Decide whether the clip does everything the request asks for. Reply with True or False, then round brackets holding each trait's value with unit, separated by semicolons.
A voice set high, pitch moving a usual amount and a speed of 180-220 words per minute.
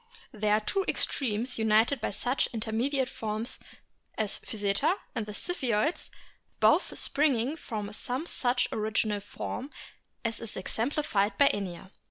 False (225 Hz; 3.9 semitones; 135 wpm)